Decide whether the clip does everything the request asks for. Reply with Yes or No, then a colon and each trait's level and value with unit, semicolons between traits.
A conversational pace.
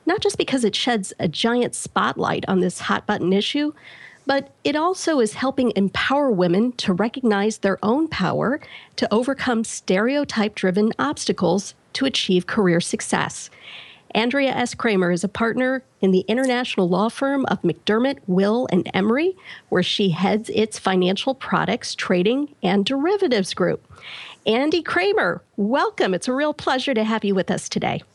Yes: average, 155 wpm